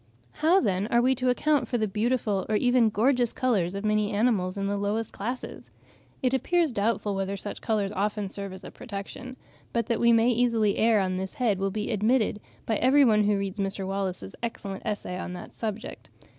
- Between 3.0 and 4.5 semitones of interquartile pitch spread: Yes, average, 3.5 semitones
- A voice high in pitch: Yes, high, 215 Hz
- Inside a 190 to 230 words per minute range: Yes, average, 200 wpm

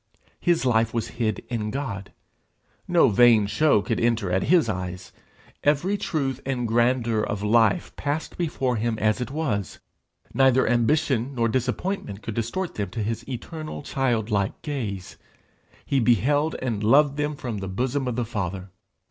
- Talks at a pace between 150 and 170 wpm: Yes, average, 155 wpm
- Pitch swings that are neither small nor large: Yes, average, 4.5 semitones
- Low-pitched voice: Yes, low, 120 Hz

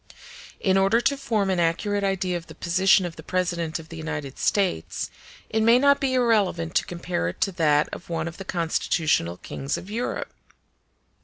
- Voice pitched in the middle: Yes, medium, 180 Hz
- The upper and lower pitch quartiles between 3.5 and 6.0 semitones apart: Yes, average, 3.8 semitones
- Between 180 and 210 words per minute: Yes, average, 185 wpm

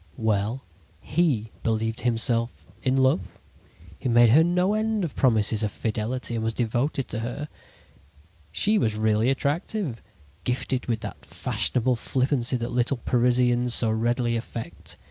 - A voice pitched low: Yes, low, 120 Hz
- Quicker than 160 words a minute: No, average, 140 wpm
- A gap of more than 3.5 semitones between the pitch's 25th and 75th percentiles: No, average, 3.0 semitones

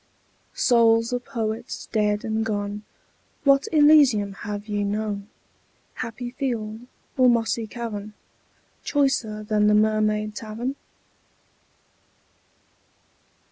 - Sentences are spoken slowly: Yes, slow, 95 wpm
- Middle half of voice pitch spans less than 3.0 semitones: Yes, narrow, 2.5 semitones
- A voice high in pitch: Yes, high, 220 Hz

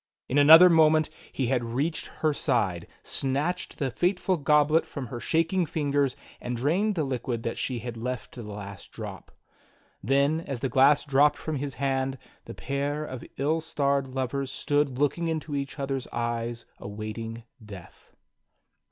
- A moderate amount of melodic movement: Yes, average, 3.8 semitones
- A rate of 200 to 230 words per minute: No, average, 160 wpm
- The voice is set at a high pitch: No, medium, 140 Hz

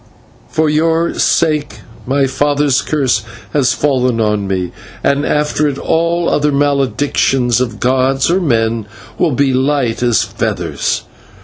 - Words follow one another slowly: Yes, slow, 130 wpm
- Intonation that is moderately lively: Yes, average, 3.3 semitones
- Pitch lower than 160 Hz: Yes, medium, 140 Hz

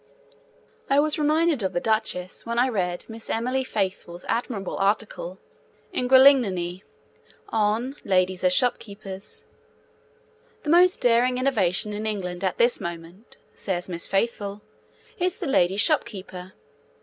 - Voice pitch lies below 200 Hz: No, high, 210 Hz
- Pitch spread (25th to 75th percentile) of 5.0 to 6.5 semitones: Yes, average, 5.3 semitones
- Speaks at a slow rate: Yes, slow, 125 wpm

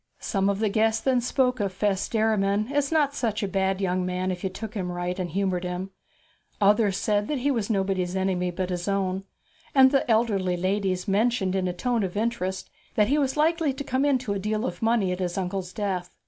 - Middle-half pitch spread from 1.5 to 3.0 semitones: No, average, 3.9 semitones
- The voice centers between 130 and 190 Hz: No, high, 200 Hz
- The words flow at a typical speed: No, fast, 215 wpm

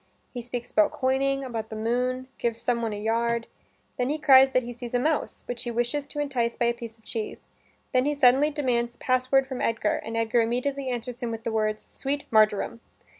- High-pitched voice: Yes, high, 245 Hz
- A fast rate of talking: Yes, fast, 220 wpm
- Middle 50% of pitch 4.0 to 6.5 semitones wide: No, narrow, 2.4 semitones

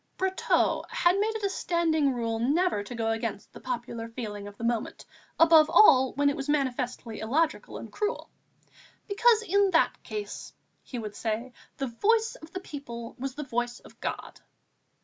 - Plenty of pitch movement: Yes, wide, 7.1 semitones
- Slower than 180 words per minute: Yes, average, 170 wpm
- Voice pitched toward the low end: No, very high, 270 Hz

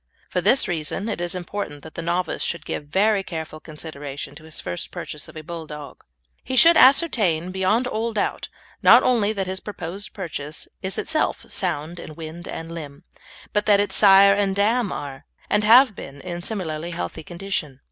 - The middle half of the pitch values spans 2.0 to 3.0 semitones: No, average, 4.7 semitones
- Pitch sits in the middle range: Yes, medium, 175 Hz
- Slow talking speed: No, average, 180 wpm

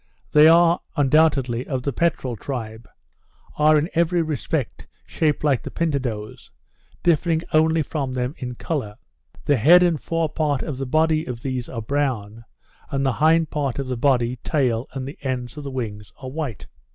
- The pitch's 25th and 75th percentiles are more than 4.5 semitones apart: No, average, 4.0 semitones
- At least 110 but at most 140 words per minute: No, average, 175 wpm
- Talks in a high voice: No, medium, 140 Hz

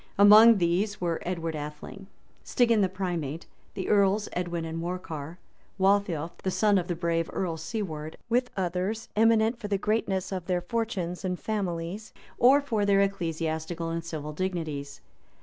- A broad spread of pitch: No, average, 3.7 semitones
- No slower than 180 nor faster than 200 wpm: No, average, 150 wpm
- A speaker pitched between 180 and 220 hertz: Yes, medium, 185 Hz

